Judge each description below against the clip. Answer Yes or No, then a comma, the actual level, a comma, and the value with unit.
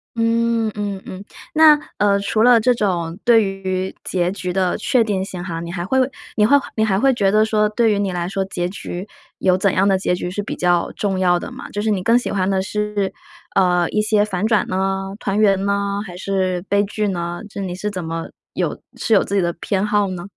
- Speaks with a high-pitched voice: Yes, high, 195 Hz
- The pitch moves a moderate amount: No, narrow, 2.3 semitones